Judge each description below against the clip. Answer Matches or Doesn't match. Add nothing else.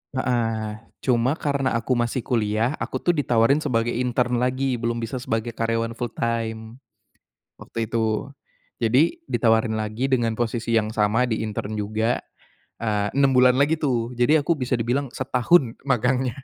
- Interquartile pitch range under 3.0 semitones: Matches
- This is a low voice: Matches